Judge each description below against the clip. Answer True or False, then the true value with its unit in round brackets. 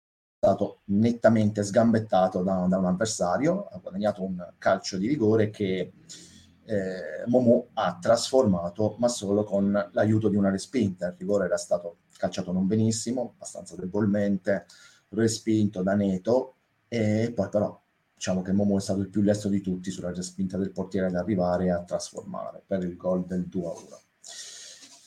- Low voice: True (100 Hz)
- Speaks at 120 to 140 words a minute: False (155 wpm)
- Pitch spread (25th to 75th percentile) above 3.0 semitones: False (2.6 semitones)